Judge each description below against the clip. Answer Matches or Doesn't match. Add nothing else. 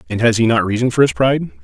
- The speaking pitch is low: Matches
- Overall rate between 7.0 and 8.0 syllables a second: Matches